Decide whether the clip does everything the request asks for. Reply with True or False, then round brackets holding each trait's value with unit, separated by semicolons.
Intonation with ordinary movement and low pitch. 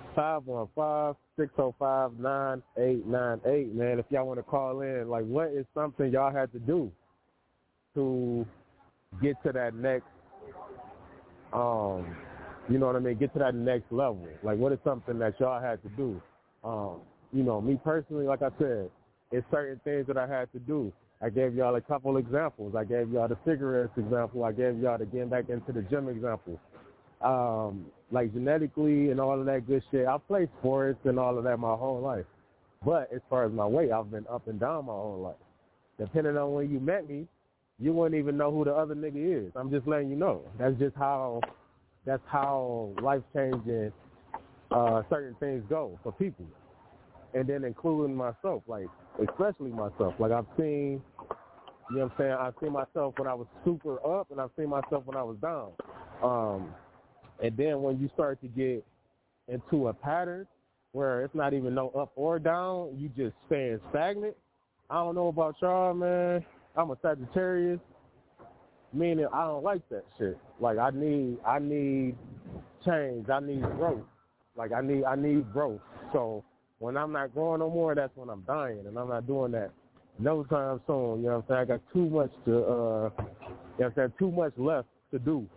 True (3.5 semitones; 130 Hz)